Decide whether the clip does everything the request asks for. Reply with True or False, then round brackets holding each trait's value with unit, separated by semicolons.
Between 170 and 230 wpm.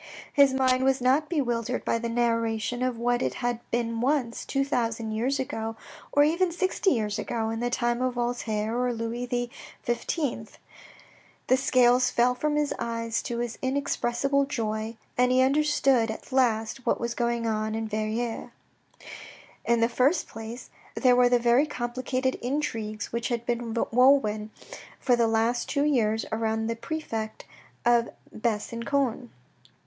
False (155 wpm)